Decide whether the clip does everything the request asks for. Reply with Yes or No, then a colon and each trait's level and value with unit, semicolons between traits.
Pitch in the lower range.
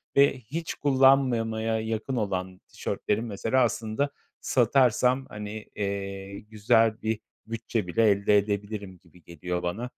Yes: low, 110 Hz